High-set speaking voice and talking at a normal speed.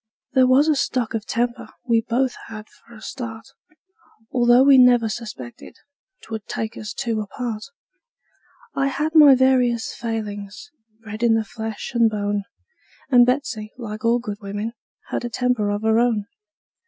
Yes: high, 230 Hz; average, 155 wpm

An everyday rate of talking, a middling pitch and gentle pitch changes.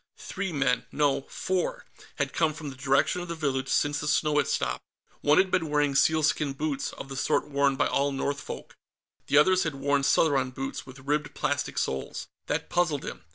Yes: average, 195 wpm; medium, 145 Hz; narrow, 2.3 semitones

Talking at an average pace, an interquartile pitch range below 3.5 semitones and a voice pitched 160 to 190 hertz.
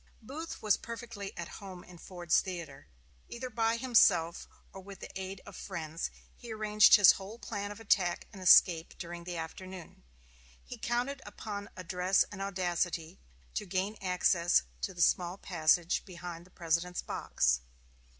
Yes: average, 150 wpm; average, 3.0 semitones; medium, 185 Hz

